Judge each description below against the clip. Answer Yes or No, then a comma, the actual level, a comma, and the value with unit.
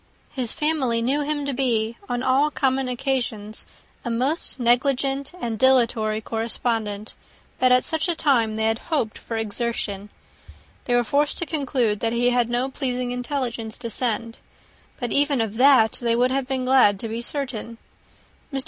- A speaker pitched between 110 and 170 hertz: No, high, 245 Hz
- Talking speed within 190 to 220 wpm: No, average, 165 wpm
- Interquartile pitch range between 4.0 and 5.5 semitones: No, average, 3.0 semitones